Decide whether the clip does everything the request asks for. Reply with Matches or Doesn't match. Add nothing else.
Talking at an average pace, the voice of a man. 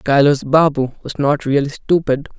Matches